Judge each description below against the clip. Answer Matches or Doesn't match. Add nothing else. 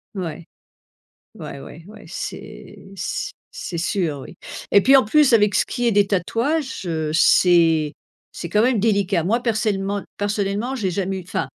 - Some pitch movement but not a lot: Matches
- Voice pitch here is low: Doesn't match